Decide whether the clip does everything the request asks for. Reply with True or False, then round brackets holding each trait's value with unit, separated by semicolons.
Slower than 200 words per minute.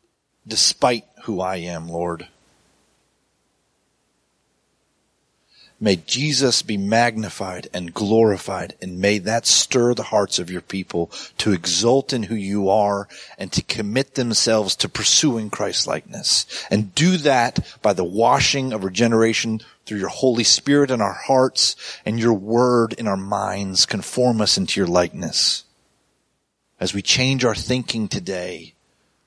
True (135 wpm)